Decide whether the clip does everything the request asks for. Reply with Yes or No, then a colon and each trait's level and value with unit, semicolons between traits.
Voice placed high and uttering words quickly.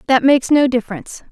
No: very high, 260 Hz; average, 185 wpm